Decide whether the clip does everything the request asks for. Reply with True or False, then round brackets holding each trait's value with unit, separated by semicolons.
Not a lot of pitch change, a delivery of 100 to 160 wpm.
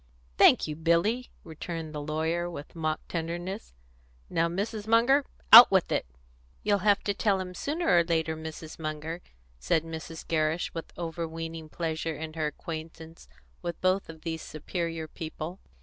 True (2.3 semitones; 150 wpm)